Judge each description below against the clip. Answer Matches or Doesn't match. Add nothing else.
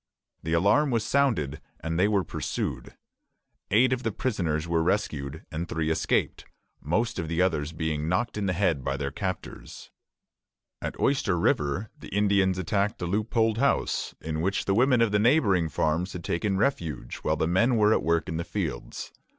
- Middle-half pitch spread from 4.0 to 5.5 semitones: Matches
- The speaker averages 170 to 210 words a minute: Matches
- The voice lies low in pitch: Matches